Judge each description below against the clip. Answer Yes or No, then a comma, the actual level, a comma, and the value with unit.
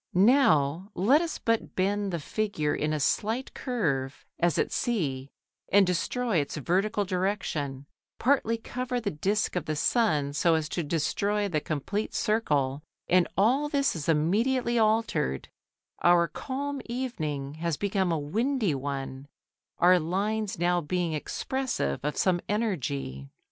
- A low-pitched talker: No, medium, 185 Hz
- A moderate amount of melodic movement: No, wide, 6.9 semitones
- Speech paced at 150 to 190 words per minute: No, average, 140 wpm